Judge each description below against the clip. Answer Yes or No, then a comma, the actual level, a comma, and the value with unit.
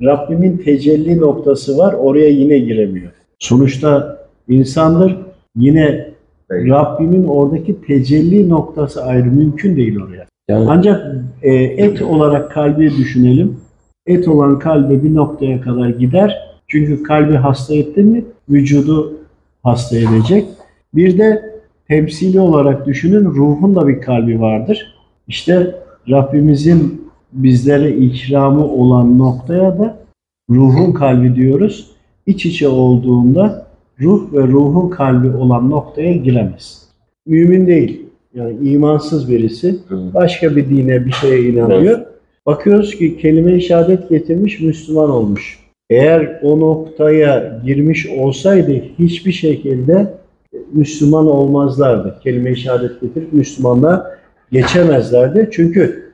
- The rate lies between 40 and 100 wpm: No, average, 110 wpm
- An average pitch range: Yes, average, 4.6 semitones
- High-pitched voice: No, medium, 150 Hz